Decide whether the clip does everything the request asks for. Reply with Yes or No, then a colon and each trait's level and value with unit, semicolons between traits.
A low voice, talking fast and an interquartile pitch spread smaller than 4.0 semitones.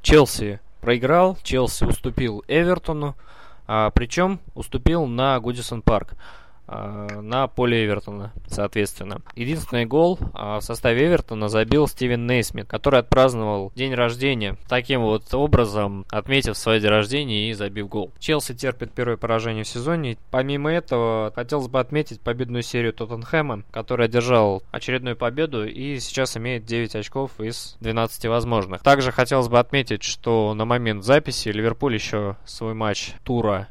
No: low, 120 Hz; average, 135 wpm; average, 3.5 semitones